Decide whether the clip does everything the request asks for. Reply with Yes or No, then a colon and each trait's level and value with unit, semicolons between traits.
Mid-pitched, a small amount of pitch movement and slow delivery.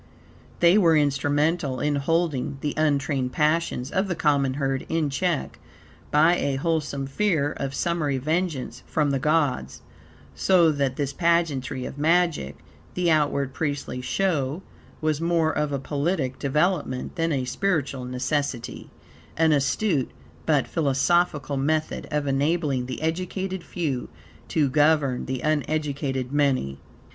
No: medium, 145 Hz; average, 3.3 semitones; slow, 130 wpm